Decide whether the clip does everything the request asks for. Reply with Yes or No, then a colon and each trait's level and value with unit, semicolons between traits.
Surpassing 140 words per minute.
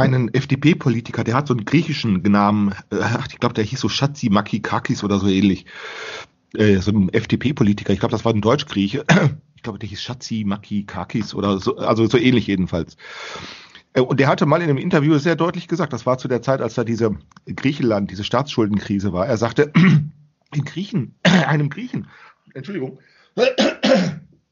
Yes: average, 170 wpm